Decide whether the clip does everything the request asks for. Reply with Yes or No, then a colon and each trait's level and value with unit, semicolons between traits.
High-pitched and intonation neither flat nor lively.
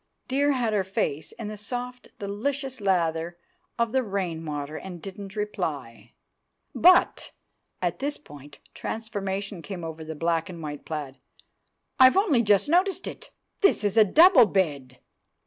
No: high, 200 Hz; wide, 7.1 semitones